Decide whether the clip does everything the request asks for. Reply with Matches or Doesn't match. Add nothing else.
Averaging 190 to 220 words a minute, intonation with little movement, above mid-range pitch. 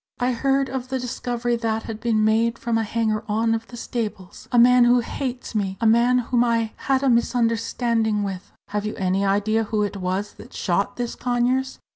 Matches